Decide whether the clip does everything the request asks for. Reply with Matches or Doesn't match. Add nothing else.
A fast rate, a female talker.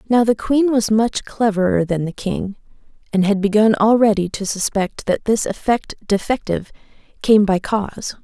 Doesn't match